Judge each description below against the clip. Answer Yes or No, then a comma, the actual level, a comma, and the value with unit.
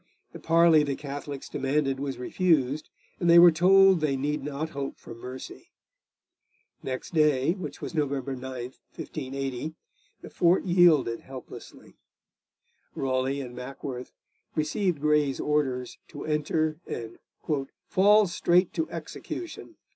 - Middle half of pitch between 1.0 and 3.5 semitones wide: No, average, 3.9 semitones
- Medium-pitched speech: Yes, medium, 145 Hz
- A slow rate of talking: Yes, slow, 125 wpm